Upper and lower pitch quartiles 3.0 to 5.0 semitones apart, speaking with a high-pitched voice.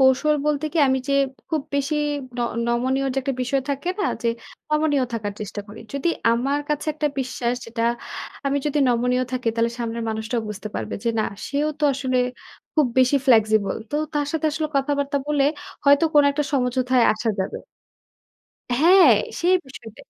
Yes: average, 3.7 semitones; very high, 265 Hz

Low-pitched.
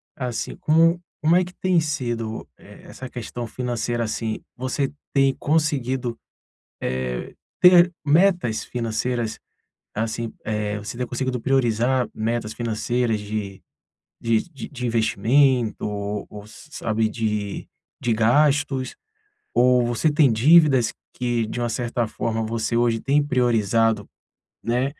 Yes: low, 120 Hz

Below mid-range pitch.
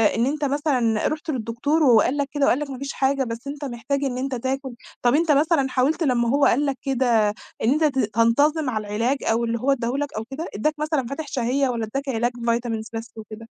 No: very high, 265 Hz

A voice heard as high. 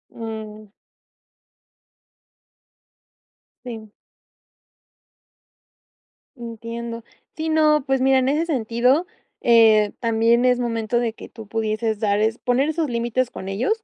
Yes: high, 235 Hz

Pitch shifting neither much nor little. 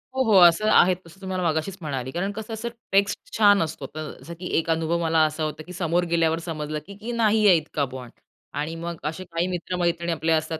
Yes: average, 3.5 semitones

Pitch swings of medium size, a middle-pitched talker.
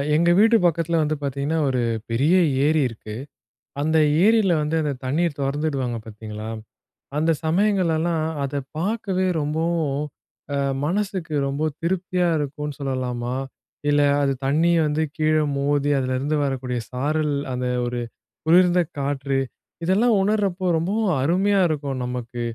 Yes: average, 4.1 semitones; medium, 150 Hz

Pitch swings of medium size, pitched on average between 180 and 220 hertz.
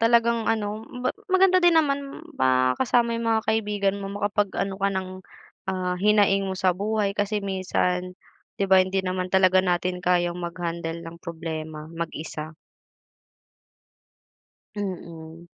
Yes: average, 3.6 semitones; high, 190 Hz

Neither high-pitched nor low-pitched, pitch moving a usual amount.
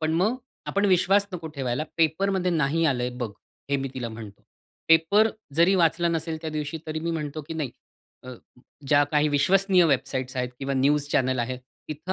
Yes: medium, 155 Hz; average, 4.1 semitones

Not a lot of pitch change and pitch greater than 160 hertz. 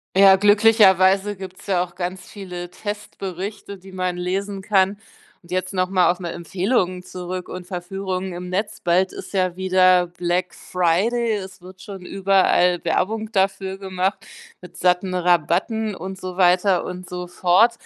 Yes: narrow, 1.5 semitones; medium, 185 Hz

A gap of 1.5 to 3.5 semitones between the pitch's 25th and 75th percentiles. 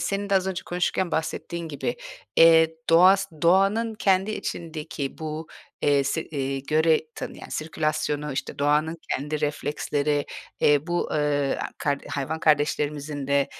Yes: average, 2.9 semitones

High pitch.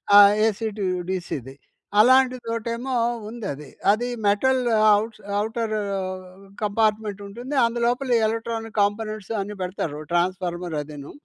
Yes: high, 215 Hz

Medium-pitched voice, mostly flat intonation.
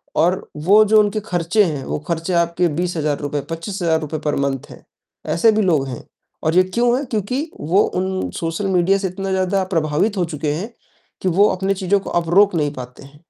No: medium, 180 Hz; average, 4.0 semitones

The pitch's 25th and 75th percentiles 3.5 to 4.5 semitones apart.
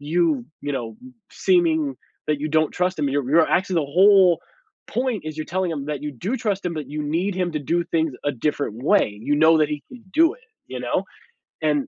Yes: average, 4.0 semitones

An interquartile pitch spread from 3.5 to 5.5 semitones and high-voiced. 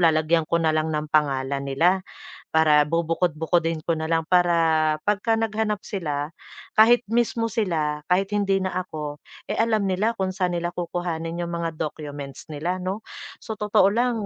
No: average, 4.0 semitones; medium, 170 Hz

